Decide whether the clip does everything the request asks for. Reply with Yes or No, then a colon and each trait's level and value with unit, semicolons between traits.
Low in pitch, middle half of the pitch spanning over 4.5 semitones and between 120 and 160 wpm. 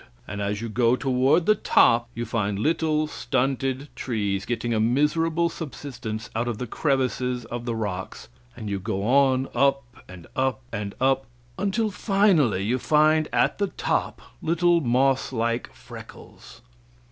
Yes: low, 125 Hz; average, 4.9 semitones; average, 150 wpm